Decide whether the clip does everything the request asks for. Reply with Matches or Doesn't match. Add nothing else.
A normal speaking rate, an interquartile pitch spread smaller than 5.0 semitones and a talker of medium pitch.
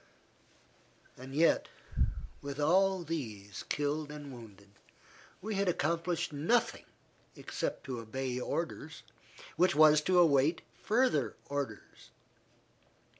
Doesn't match